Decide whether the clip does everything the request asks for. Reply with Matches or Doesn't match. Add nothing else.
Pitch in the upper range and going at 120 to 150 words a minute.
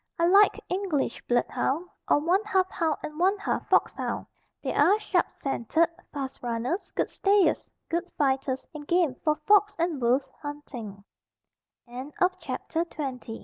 Matches